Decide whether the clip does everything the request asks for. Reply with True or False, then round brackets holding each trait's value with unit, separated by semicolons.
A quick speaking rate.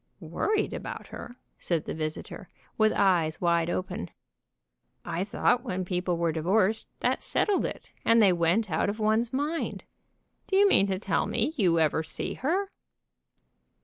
False (155 wpm)